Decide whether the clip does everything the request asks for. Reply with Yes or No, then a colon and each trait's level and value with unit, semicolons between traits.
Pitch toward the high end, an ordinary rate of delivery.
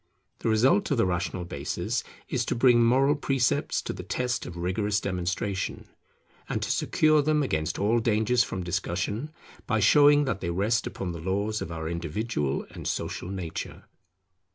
No: low, 105 Hz; average, 165 wpm